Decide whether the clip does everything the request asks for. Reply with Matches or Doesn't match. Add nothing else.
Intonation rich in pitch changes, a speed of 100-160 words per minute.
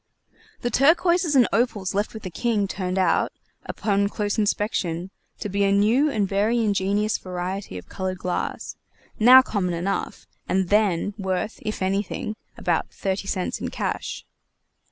Doesn't match